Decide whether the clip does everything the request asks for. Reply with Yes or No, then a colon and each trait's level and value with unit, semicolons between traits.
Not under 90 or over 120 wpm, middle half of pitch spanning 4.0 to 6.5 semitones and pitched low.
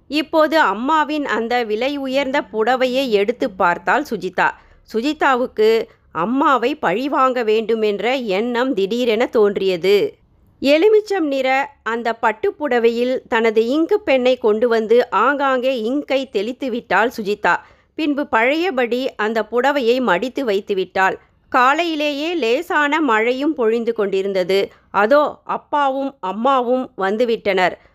No: average, 100 wpm; average, 4.7 semitones; very high, 250 Hz